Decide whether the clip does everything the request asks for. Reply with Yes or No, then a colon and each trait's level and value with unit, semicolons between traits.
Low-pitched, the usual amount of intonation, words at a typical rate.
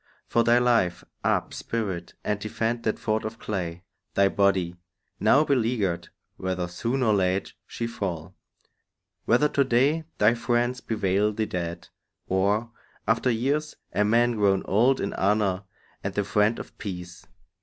Yes: low, 105 Hz; average, 3.8 semitones; average, 145 wpm